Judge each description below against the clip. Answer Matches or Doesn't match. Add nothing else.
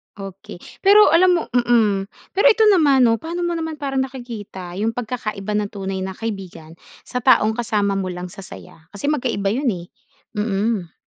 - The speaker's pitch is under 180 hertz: Doesn't match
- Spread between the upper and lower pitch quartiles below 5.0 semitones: Doesn't match